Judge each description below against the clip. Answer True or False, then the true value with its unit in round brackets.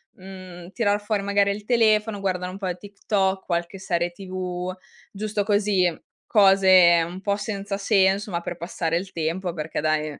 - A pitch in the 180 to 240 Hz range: True (190 Hz)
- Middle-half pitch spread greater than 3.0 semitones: False (2.5 semitones)